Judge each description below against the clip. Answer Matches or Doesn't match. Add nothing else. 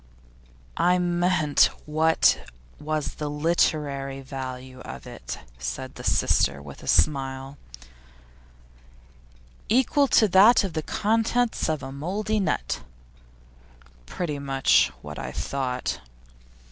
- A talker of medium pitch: Matches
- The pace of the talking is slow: Matches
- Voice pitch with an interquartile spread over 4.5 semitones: Matches